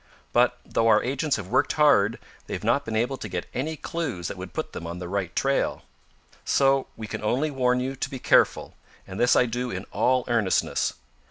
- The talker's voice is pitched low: Yes, low, 120 Hz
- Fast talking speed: Yes, fast, 210 wpm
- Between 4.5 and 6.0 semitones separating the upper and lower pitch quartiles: Yes, average, 5.1 semitones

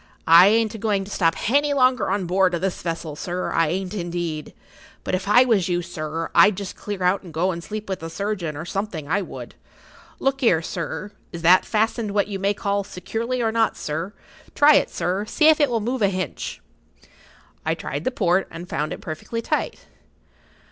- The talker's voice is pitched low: No, high, 190 Hz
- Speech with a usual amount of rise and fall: Yes, average, 4.0 semitones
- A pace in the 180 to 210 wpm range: Yes, fast, 205 wpm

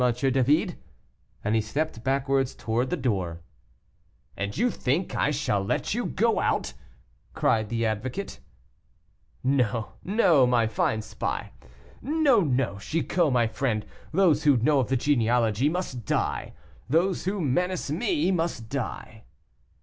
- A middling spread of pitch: No, wide, 6.7 semitones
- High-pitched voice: No, low, 135 Hz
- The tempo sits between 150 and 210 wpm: No, slow, 135 wpm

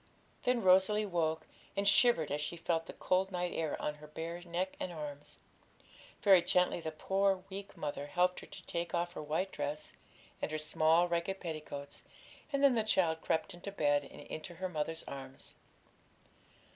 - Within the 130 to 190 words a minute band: Yes, average, 175 wpm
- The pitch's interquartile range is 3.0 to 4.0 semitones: Yes, average, 3.5 semitones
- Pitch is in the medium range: Yes, medium, 170 Hz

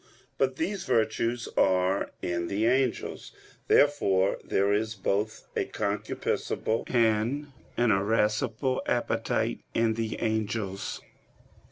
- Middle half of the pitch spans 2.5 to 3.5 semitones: Yes, average, 3.0 semitones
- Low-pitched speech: Yes, low, 110 Hz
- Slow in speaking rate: Yes, slow, 100 wpm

